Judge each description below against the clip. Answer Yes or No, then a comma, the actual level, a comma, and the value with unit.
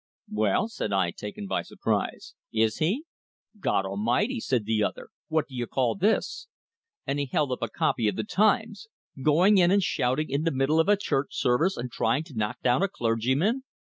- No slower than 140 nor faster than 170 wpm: No, average, 195 wpm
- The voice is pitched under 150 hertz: Yes, low, 135 Hz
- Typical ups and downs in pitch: No, wide, 8.6 semitones